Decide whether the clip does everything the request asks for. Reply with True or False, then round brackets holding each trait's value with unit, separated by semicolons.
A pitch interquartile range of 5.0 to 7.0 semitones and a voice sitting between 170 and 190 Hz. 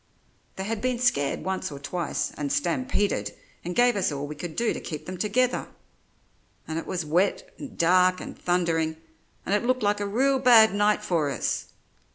True (5.3 semitones; 185 Hz)